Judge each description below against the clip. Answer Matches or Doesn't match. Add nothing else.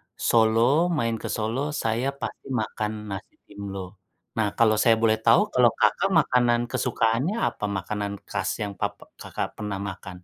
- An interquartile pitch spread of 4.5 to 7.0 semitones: Doesn't match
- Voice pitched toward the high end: Doesn't match